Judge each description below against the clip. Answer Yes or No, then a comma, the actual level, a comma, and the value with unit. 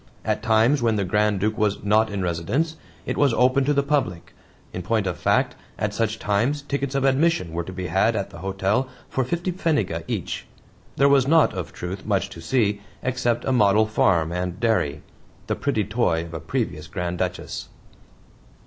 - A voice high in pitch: No, low, 105 Hz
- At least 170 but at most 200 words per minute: Yes, average, 190 wpm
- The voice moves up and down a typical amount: No, wide, 6.3 semitones